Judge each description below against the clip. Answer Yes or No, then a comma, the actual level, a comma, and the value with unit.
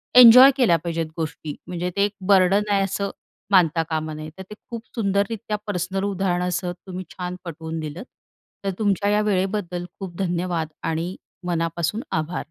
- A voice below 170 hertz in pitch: No, medium, 180 Hz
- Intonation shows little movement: No, average, 3.1 semitones